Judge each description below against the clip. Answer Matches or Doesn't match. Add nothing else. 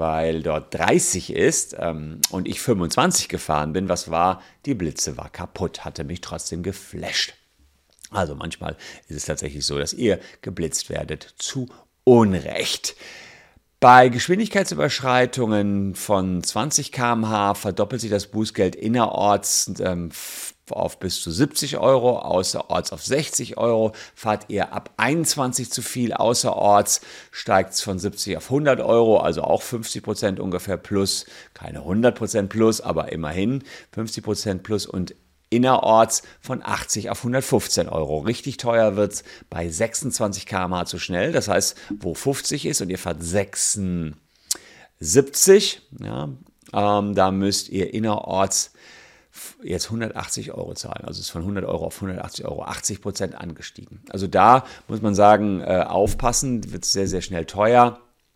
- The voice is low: Matches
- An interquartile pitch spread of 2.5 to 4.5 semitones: Doesn't match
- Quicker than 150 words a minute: Doesn't match